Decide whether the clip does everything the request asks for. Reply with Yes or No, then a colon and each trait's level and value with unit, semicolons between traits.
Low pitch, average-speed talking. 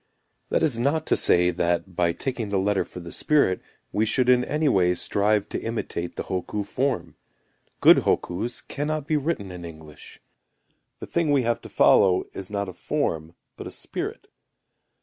Yes: low, 100 Hz; average, 175 wpm